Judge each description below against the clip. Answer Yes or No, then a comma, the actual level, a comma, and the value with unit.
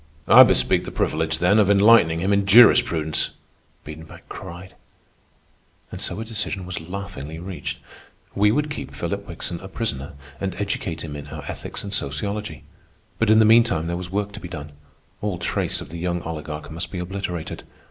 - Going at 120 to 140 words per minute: No, average, 180 wpm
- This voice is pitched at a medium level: No, very low, 90 Hz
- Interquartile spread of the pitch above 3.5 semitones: Yes, average, 4.0 semitones